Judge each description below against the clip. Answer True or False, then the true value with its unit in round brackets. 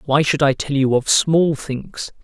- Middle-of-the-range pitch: True (145 Hz)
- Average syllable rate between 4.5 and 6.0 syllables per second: False (3.9 syllables/s)